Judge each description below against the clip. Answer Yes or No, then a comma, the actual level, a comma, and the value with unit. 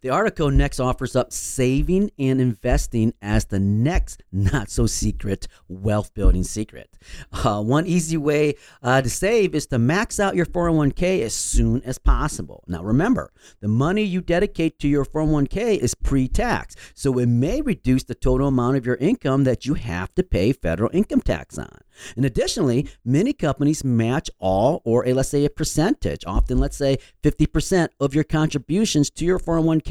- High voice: No, low, 135 Hz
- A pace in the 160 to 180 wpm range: Yes, average, 175 wpm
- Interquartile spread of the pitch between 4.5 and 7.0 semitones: Yes, average, 4.9 semitones